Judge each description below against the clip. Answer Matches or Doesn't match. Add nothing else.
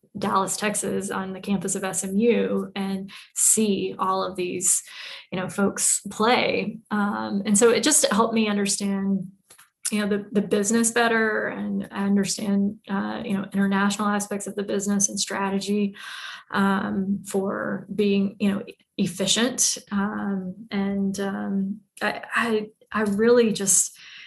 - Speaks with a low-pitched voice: Doesn't match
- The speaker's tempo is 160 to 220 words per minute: Doesn't match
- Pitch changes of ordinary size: Doesn't match